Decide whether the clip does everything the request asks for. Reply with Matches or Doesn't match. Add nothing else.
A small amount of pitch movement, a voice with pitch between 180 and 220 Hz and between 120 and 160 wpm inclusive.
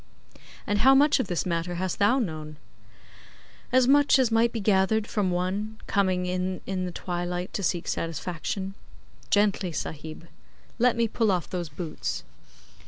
Doesn't match